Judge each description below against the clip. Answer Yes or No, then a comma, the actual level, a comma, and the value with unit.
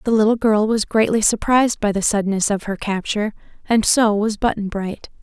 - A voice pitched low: No, high, 215 Hz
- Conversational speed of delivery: Yes, average, 195 wpm